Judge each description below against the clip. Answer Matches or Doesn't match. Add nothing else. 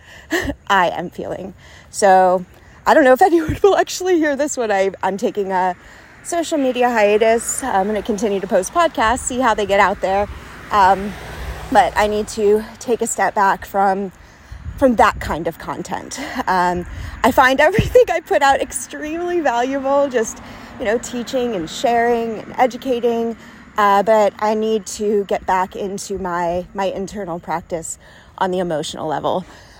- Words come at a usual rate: Matches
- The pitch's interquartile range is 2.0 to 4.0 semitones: Doesn't match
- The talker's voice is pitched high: Matches